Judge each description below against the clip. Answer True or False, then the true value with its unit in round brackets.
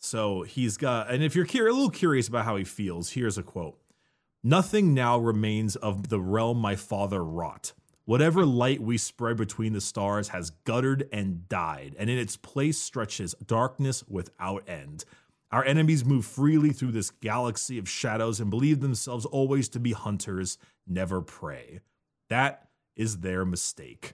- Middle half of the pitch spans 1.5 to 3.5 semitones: False (4.8 semitones)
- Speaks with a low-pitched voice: True (115 Hz)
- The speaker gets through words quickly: False (165 wpm)